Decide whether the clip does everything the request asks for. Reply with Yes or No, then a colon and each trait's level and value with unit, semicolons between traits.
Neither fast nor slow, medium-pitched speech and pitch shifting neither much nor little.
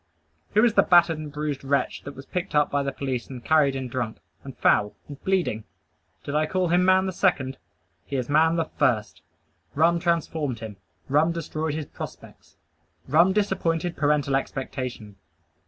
Yes: average, 170 wpm; medium, 150 Hz; average, 4.0 semitones